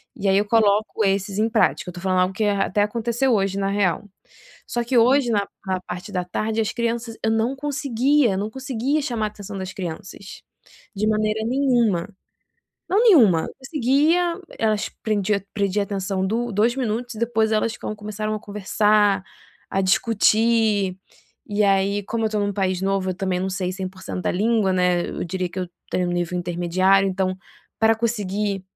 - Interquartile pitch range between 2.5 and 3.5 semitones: Yes, average, 3.2 semitones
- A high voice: Yes, high, 210 Hz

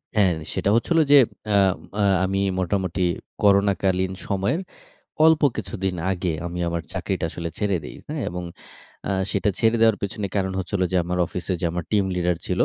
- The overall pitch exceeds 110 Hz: No, very low, 95 Hz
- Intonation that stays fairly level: Yes, narrow, 2.2 semitones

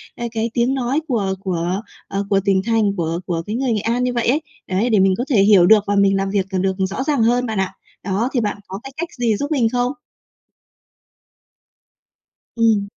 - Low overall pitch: No, high, 215 Hz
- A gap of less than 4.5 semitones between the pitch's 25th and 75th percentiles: Yes, average, 4.0 semitones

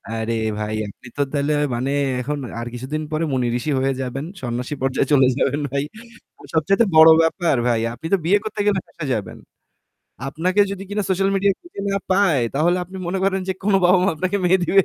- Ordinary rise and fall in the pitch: No, wide, 6.3 semitones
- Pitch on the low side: No, medium, 160 Hz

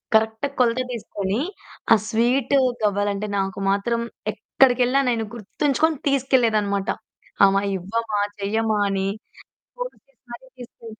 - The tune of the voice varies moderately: Yes, average, 3.7 semitones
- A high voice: Yes, high, 225 Hz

